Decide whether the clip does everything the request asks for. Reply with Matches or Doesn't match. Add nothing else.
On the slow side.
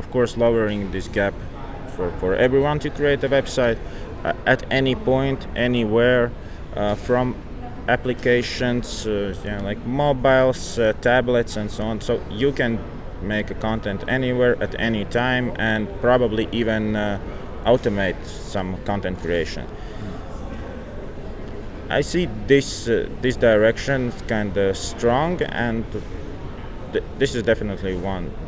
Matches